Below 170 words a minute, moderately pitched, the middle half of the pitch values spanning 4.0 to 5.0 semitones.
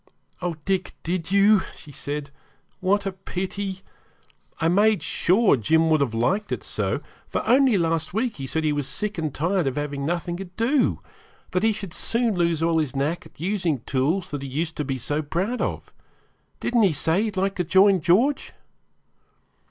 No: average, 185 wpm; medium, 175 Hz; average, 4.7 semitones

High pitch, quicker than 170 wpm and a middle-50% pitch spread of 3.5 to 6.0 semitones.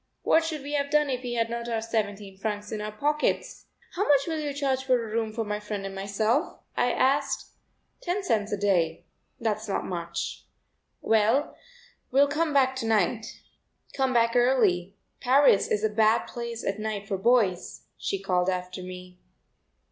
Yes: high, 225 Hz; average, 180 wpm; average, 4.6 semitones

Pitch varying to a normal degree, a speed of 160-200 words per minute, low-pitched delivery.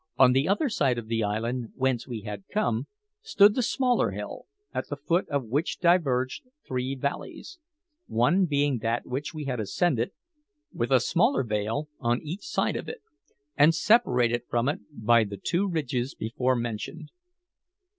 No: wide, 5.8 semitones; average, 165 wpm; low, 130 Hz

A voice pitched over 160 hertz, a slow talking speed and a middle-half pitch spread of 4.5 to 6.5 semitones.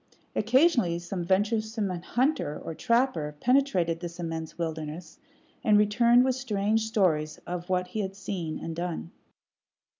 Yes: high, 190 Hz; slow, 130 wpm; average, 4.9 semitones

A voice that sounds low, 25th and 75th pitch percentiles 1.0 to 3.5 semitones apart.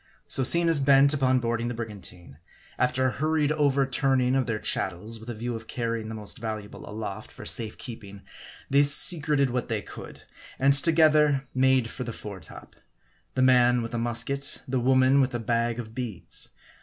Yes: low, 125 Hz; average, 3.2 semitones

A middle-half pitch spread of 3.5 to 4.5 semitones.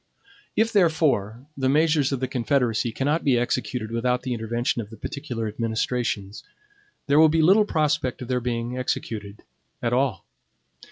Yes: average, 3.8 semitones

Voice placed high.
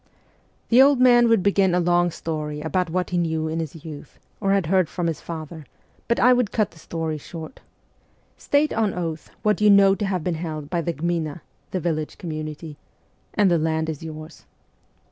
No: medium, 170 Hz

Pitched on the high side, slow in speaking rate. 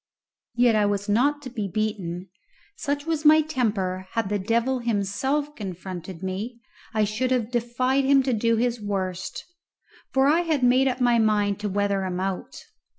No: high, 225 Hz; average, 170 wpm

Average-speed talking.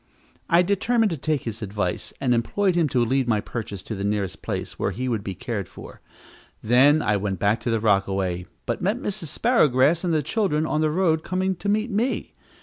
No: fast, 210 wpm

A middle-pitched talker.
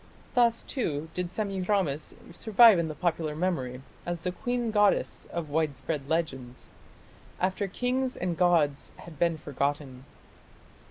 Yes: medium, 170 Hz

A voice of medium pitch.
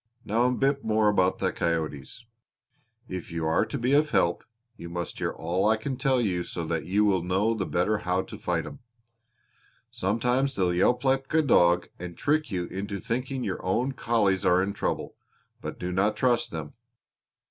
No: low, 100 Hz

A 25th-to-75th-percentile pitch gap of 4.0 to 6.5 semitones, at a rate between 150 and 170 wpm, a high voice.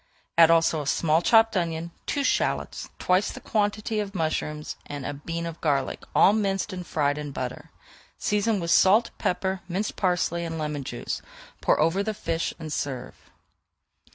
No: average, 4.5 semitones; average, 165 wpm; medium, 170 Hz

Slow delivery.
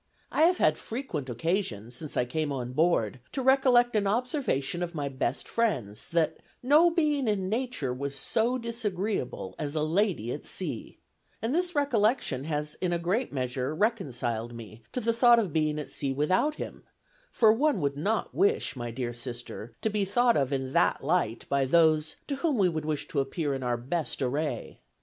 No: average, 185 wpm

